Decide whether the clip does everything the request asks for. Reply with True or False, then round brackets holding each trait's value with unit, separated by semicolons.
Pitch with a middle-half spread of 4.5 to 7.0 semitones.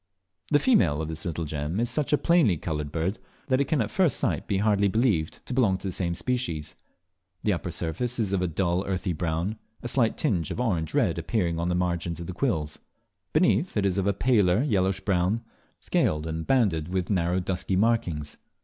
True (5.2 semitones)